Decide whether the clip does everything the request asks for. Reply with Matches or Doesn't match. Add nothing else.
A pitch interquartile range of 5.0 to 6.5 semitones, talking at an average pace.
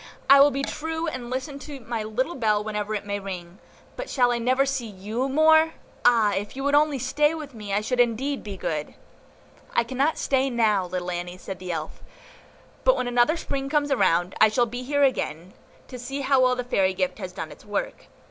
Doesn't match